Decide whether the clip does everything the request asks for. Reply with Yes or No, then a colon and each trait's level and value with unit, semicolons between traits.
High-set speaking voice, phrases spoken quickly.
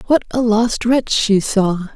No: high, 225 Hz; average, 185 wpm